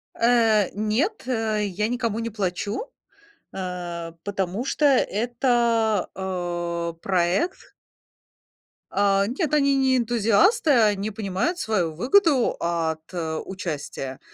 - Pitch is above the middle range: Yes, high, 210 Hz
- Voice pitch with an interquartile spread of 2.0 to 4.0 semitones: No, average, 5.1 semitones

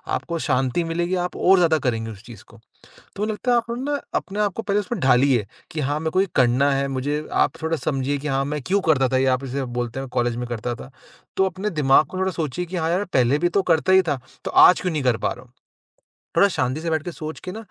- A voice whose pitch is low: No, medium, 150 Hz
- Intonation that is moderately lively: No, wide, 5.8 semitones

